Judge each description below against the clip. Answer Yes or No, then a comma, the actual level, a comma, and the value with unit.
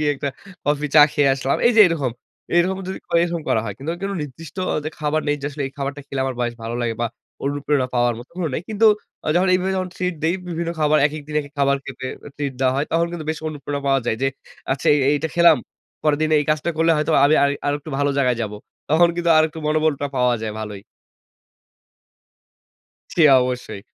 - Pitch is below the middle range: No, medium, 145 Hz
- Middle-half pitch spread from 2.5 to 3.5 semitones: Yes, average, 3.2 semitones